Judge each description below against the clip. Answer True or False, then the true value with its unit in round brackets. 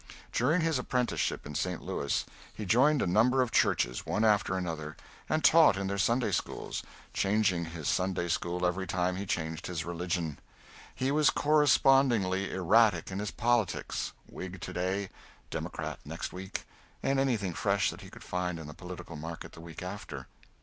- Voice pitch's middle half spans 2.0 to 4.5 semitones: False (5.2 semitones)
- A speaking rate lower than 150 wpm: False (170 wpm)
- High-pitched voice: False (95 Hz)